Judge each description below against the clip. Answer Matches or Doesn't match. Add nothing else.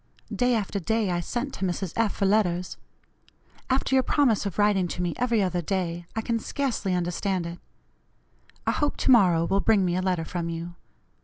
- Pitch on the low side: Doesn't match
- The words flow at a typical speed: Matches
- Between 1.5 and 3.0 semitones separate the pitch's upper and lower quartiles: Doesn't match